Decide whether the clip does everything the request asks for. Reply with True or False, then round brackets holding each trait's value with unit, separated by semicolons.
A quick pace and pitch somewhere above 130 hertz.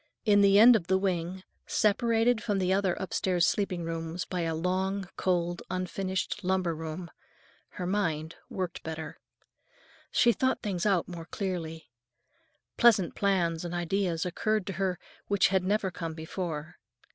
False (145 wpm; 185 Hz)